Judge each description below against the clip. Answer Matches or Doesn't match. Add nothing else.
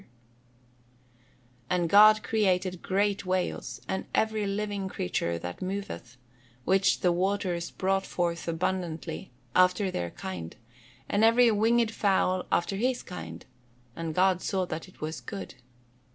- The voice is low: Doesn't match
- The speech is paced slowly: Matches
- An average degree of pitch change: Matches